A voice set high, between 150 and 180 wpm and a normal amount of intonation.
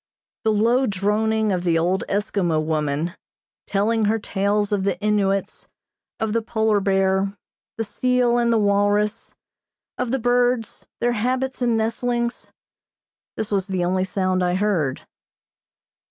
No: high, 210 Hz; average, 140 wpm; average, 3.0 semitones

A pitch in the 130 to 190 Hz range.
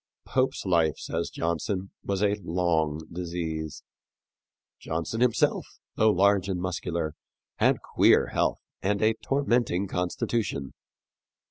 No: very low, 90 Hz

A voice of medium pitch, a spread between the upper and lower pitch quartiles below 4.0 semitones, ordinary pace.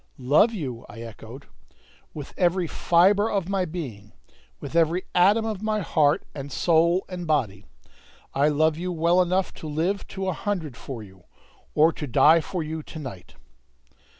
No: medium, 160 Hz; average, 4.6 semitones; average, 165 wpm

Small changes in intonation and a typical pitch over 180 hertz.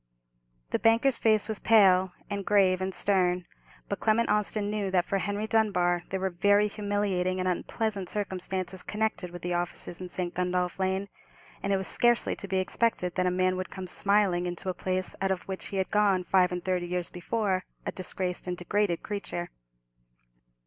Yes: narrow, 2.1 semitones; high, 190 Hz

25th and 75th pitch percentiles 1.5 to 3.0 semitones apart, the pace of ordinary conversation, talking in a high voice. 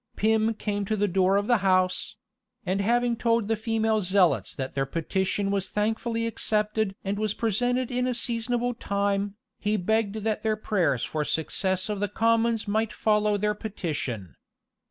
Yes: narrow, 2.5 semitones; average, 170 wpm; high, 210 Hz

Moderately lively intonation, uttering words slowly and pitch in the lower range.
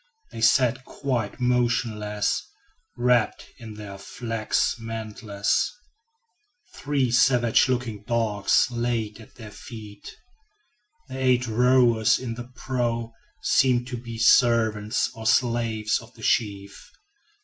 No: narrow, 2.2 semitones; slow, 110 wpm; low, 115 Hz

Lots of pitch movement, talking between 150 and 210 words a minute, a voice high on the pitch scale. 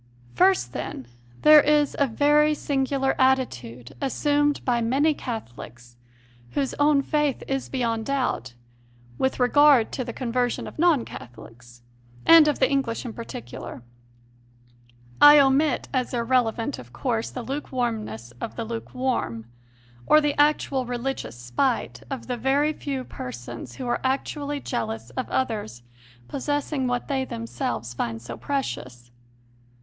No: wide, 6.5 semitones; slow, 135 wpm; very high, 255 Hz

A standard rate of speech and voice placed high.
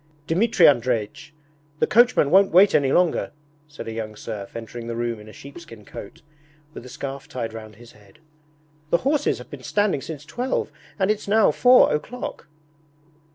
No: average, 170 wpm; medium, 140 Hz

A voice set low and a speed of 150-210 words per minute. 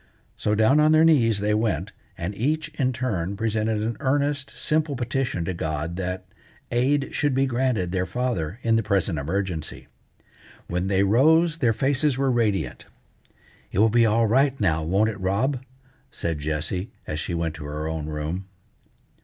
Yes: low, 110 Hz; average, 170 wpm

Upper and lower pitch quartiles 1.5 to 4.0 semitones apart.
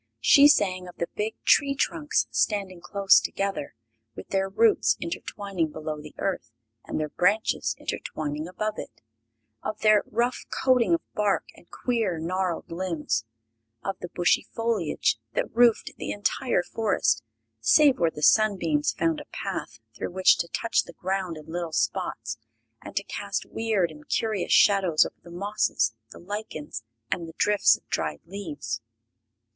No: average, 4.9 semitones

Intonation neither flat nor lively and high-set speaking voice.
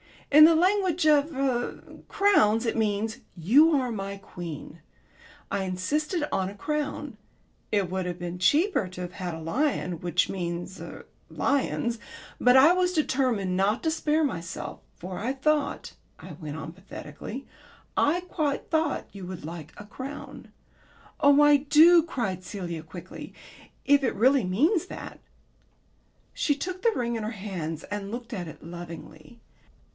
No: wide, 8.3 semitones; high, 225 Hz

